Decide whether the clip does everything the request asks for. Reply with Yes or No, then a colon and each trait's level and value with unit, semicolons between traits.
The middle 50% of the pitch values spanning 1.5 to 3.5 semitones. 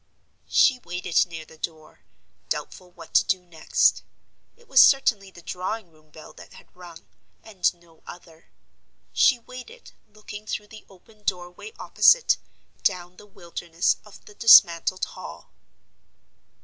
No: average, 3.9 semitones